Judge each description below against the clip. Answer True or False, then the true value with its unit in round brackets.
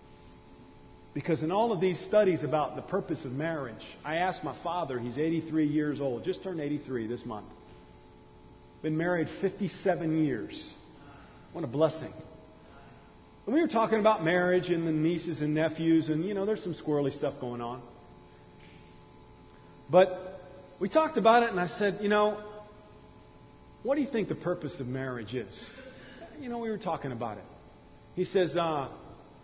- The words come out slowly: False (165 wpm)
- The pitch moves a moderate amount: False (5.7 semitones)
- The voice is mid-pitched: True (160 Hz)